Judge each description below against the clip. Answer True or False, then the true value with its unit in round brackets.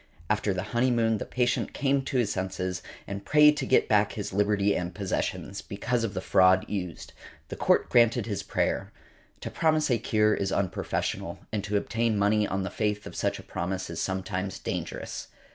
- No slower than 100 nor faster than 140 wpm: False (185 wpm)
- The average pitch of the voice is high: False (105 Hz)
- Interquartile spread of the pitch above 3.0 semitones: True (3.4 semitones)